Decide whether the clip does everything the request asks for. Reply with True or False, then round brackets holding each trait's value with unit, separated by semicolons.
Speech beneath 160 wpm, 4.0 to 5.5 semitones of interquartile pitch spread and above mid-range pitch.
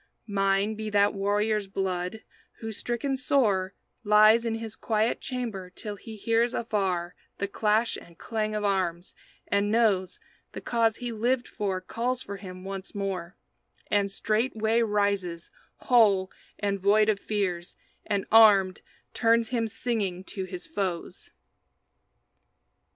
False (135 wpm; 2.7 semitones; 210 Hz)